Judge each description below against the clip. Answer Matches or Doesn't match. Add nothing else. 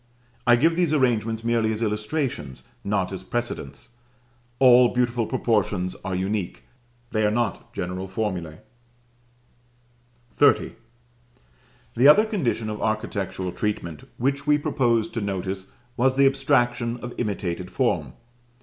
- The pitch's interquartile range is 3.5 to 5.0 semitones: Matches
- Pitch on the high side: Doesn't match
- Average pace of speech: Doesn't match